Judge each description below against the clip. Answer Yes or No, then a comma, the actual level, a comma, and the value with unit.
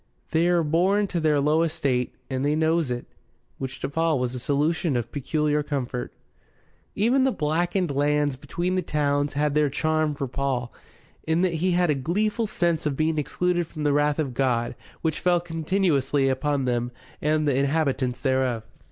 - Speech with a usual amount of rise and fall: Yes, average, 3.5 semitones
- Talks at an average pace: Yes, average, 175 wpm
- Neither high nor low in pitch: Yes, medium, 150 Hz